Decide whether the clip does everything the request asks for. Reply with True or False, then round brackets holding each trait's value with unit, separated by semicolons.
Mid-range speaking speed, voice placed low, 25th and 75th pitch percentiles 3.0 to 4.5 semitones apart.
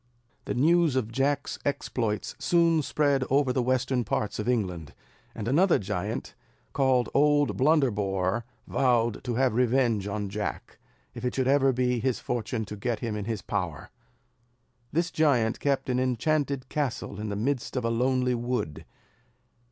True (155 wpm; 125 Hz; 3.9 semitones)